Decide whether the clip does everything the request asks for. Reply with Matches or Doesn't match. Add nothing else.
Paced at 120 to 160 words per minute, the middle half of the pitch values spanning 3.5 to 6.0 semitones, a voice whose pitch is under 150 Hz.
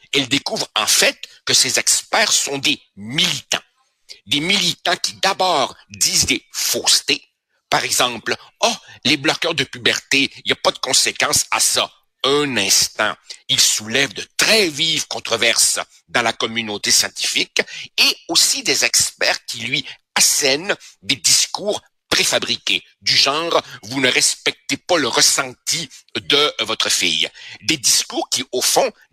Matches